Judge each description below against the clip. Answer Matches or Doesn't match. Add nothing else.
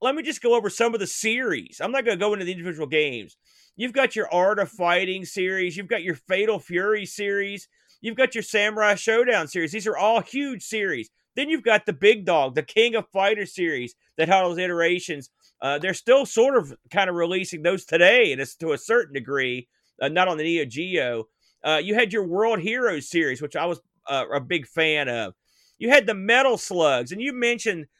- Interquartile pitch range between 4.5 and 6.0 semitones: Matches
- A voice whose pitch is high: Matches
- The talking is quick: Matches